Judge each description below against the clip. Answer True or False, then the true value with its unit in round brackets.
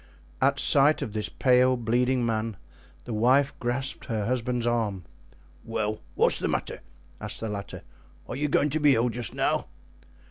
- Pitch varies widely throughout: False (2.6 semitones)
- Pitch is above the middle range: False (120 Hz)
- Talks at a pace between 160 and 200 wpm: True (165 wpm)